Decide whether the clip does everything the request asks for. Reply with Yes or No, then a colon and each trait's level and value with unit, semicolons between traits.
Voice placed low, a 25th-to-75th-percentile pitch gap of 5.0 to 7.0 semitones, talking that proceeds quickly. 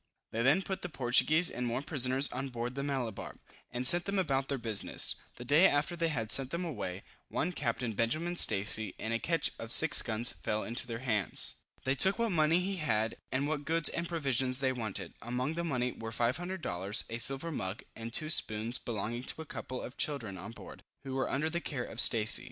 Yes: low, 130 Hz; average, 5.3 semitones; fast, 215 wpm